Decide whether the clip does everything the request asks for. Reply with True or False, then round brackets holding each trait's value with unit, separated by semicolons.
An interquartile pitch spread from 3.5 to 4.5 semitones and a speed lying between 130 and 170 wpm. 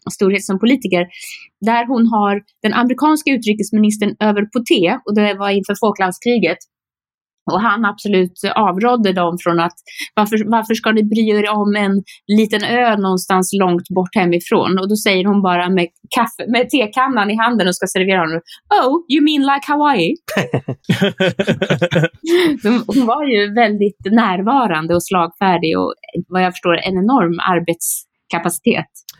True (3.9 semitones; 150 wpm)